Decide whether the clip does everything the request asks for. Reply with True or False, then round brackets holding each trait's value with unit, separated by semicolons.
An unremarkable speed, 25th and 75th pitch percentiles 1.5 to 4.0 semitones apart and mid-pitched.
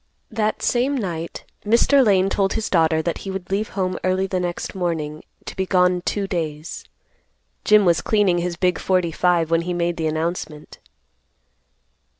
True (165 wpm; 2.5 semitones; 180 Hz)